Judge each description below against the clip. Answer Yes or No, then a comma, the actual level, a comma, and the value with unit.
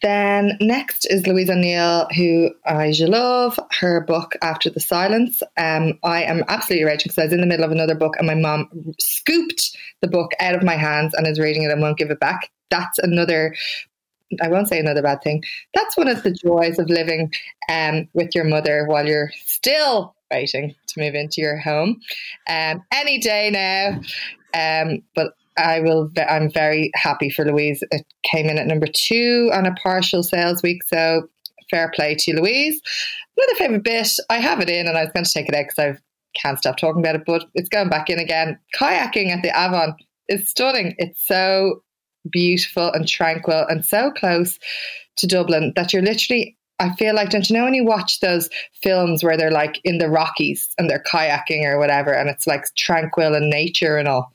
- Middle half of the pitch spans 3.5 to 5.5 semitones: Yes, average, 3.8 semitones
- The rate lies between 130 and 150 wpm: No, average, 200 wpm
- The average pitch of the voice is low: No, medium, 170 Hz